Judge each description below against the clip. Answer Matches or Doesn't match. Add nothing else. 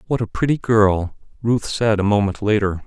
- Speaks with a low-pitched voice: Matches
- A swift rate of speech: Doesn't match